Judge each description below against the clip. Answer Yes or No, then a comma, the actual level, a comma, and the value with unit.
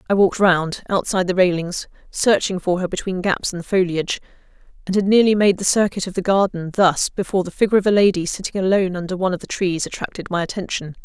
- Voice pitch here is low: No, medium, 185 Hz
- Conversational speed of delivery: No, fast, 215 wpm